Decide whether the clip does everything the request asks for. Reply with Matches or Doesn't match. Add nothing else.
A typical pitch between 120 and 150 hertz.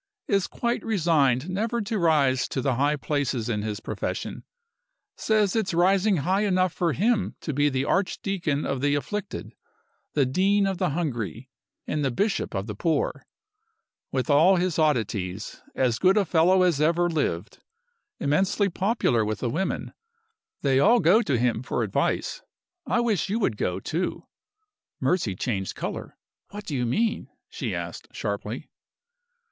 Doesn't match